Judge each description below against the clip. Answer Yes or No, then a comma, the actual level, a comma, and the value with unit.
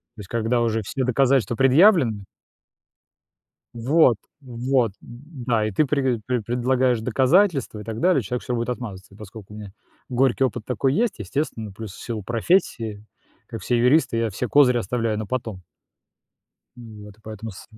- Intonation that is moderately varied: Yes, average, 3.2 semitones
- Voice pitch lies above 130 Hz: No, low, 120 Hz